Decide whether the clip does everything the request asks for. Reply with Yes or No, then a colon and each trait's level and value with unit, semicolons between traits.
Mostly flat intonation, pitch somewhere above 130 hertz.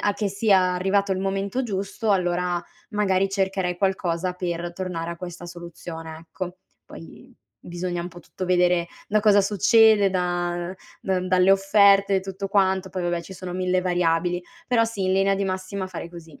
Yes: narrow, 1.9 semitones; medium, 185 Hz